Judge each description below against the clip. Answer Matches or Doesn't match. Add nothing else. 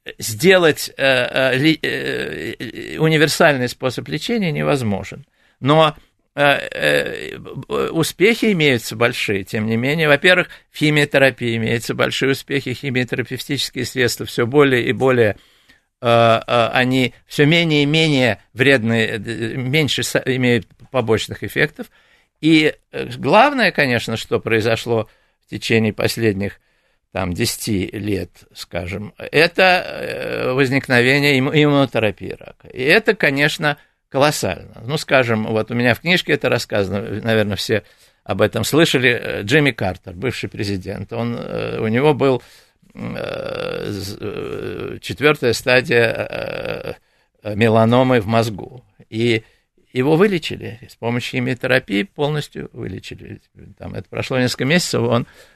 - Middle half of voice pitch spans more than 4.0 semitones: Matches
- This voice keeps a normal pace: Doesn't match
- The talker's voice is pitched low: Matches